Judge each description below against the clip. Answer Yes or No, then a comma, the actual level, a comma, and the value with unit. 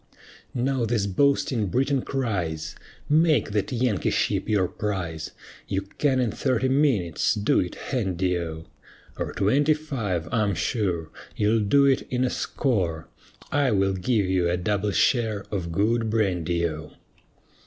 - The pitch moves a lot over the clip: Yes, wide, 6.0 semitones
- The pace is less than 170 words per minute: Yes, average, 145 wpm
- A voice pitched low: Yes, low, 105 Hz